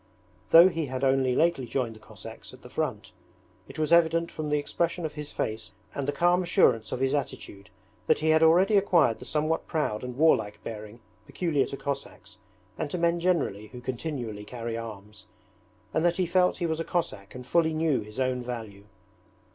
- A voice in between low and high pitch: Yes, medium, 145 Hz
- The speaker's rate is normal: Yes, average, 195 wpm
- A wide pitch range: Yes, wide, 6.0 semitones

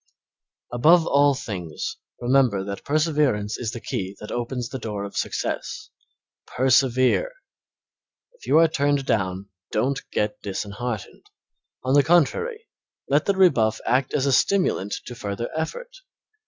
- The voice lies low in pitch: Yes, low, 130 Hz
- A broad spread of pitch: Yes, wide, 6.1 semitones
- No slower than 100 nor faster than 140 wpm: Yes, slow, 135 wpm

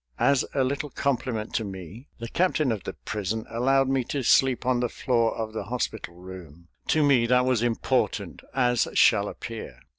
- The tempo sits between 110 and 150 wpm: No, average, 180 wpm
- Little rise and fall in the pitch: No, average, 3.4 semitones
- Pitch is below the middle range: Yes, low, 120 Hz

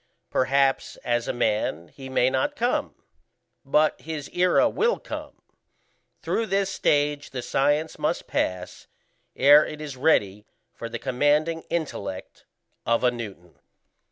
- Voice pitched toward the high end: No, medium, 140 Hz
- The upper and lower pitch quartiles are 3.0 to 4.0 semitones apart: No, average, 4.9 semitones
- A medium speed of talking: No, slow, 130 wpm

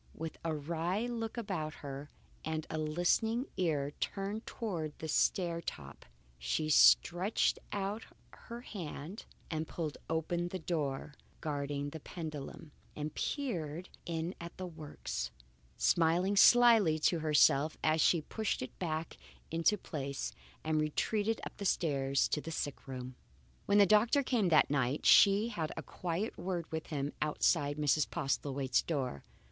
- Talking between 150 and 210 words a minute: No, average, 140 wpm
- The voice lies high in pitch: No, medium, 160 Hz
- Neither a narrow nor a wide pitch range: Yes, average, 4.2 semitones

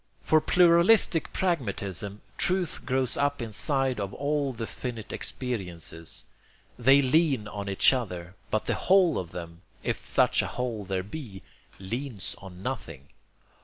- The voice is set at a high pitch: No, low, 120 Hz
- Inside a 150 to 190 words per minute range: No, slow, 135 wpm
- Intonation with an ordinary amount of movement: No, wide, 6.7 semitones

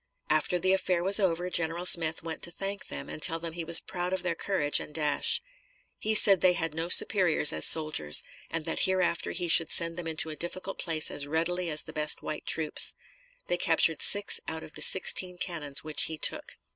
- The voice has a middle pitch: Yes, medium, 165 Hz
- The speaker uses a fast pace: Yes, fast, 210 wpm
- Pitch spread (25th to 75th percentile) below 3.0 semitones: Yes, narrow, 2.4 semitones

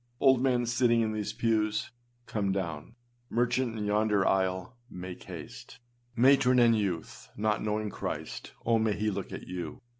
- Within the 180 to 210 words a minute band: No, average, 155 wpm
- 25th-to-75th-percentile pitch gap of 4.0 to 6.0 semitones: No, average, 3.1 semitones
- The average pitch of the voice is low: Yes, low, 110 Hz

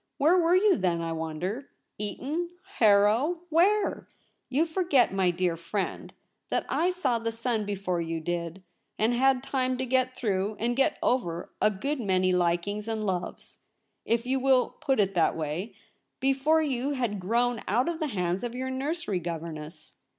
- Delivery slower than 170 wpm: No, average, 175 wpm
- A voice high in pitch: Yes, high, 230 Hz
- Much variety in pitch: Yes, wide, 6.5 semitones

